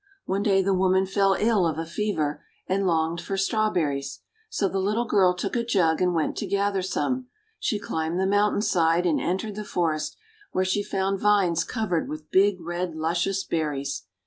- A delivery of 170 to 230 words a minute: Yes, average, 185 wpm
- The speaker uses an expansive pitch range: No, average, 3.5 semitones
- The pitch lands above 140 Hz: Yes, high, 190 Hz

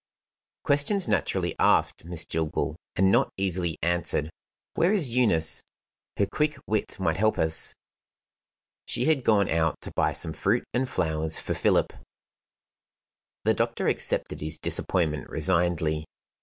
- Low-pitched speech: Yes, very low, 90 Hz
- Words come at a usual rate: No, slow, 130 wpm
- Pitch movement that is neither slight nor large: No, wide, 6.5 semitones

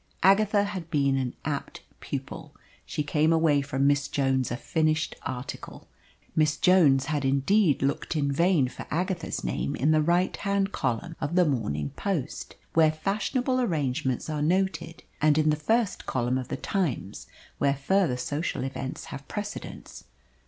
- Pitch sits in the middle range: Yes, medium, 155 Hz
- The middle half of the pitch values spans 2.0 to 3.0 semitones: No, average, 5.1 semitones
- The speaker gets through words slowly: No, average, 155 wpm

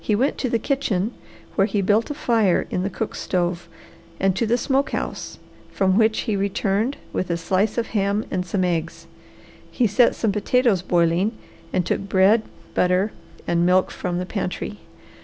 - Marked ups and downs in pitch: No, average, 3.5 semitones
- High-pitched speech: Yes, high, 195 Hz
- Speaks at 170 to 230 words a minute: Yes, average, 175 wpm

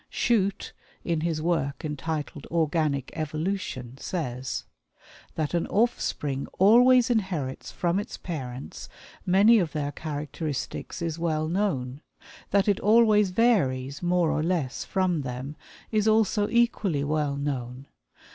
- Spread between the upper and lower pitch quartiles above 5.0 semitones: Yes, wide, 5.6 semitones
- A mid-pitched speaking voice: Yes, medium, 160 Hz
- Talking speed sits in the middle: No, slow, 120 wpm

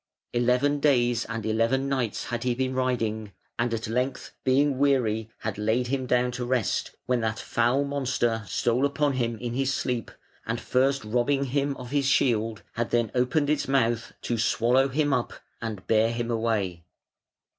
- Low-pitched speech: Yes, low, 125 Hz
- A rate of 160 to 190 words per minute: Yes, average, 170 wpm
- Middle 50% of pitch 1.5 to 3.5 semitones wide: Yes, average, 2.7 semitones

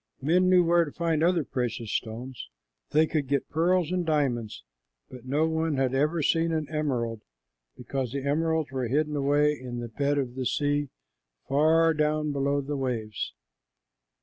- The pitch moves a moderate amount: Yes, average, 3.6 semitones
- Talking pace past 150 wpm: Yes, average, 165 wpm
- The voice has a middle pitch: Yes, medium, 145 Hz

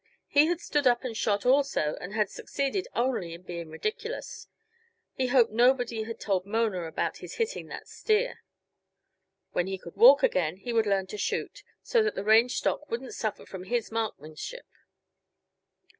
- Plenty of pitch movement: Yes, wide, 6.3 semitones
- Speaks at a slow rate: No, average, 170 wpm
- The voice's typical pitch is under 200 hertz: No, high, 230 Hz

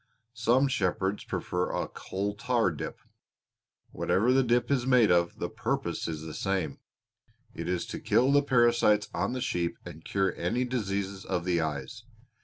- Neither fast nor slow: Yes, average, 165 wpm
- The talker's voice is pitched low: Yes, low, 100 Hz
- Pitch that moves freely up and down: Yes, wide, 5.7 semitones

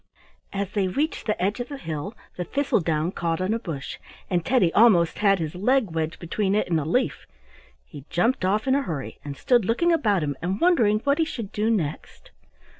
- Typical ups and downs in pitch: No, wide, 6.1 semitones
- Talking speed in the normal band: No, fast, 210 wpm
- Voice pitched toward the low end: No, high, 200 Hz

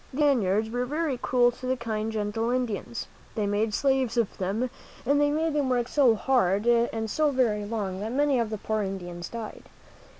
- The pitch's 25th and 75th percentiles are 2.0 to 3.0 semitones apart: No, average, 3.5 semitones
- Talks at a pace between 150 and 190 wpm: No, average, 200 wpm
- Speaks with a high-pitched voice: Yes, high, 235 Hz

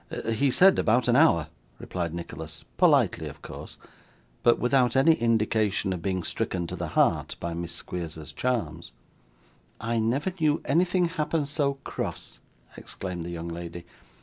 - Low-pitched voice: Yes, low, 110 Hz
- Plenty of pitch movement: Yes, wide, 8.3 semitones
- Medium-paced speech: Yes, average, 150 wpm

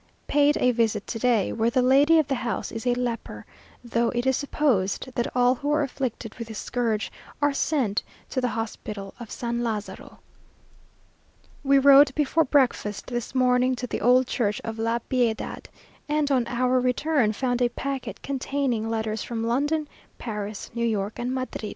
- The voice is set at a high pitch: Yes, high, 245 Hz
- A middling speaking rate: Yes, average, 175 wpm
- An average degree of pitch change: Yes, average, 3.1 semitones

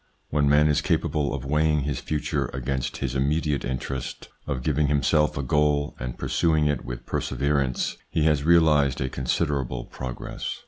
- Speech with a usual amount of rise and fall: No, narrow, 2.2 semitones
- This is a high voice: No, very low, 70 Hz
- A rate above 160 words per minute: No, average, 155 wpm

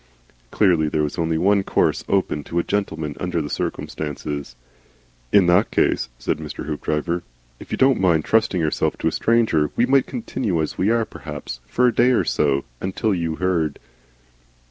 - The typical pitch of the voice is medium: No, very low, 85 Hz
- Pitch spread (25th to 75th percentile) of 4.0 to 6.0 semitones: Yes, average, 5.2 semitones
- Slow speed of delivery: No, average, 175 wpm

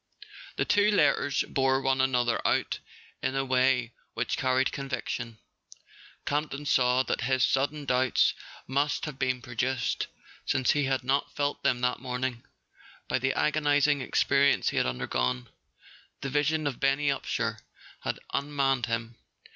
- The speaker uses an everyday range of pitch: No, narrow, 2.1 semitones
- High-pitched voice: No, low, 130 Hz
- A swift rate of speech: No, average, 145 wpm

